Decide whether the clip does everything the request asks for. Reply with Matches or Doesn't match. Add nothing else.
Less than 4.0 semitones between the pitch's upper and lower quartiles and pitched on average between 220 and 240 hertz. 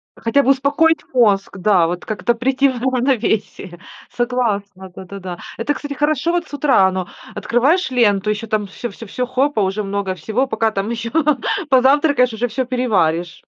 Doesn't match